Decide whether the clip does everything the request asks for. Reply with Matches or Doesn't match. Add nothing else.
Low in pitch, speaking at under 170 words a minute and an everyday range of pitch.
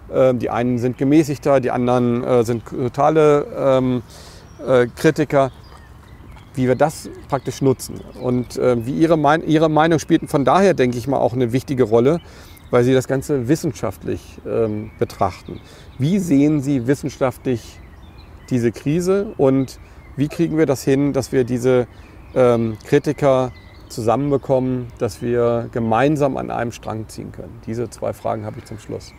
Matches